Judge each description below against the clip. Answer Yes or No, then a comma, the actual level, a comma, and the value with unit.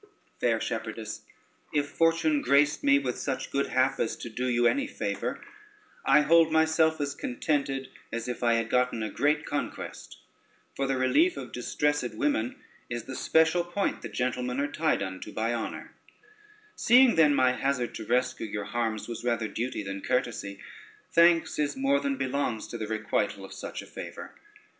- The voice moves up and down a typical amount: Yes, average, 4.4 semitones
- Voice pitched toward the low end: Yes, low, 130 Hz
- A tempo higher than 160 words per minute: Yes, average, 175 wpm